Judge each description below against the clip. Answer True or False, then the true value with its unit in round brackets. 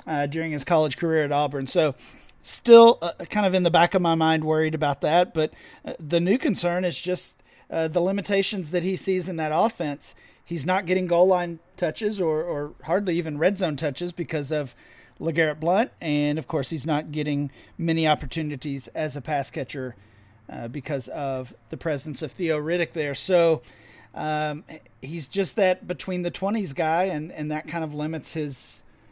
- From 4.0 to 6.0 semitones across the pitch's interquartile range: False (3.2 semitones)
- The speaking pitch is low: False (160 Hz)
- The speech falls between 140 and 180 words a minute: False (190 wpm)